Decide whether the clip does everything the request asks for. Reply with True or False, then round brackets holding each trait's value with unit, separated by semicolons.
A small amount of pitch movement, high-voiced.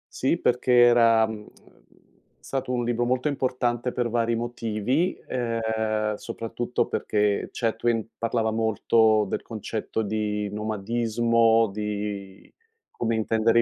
False (1.8 semitones; 115 Hz)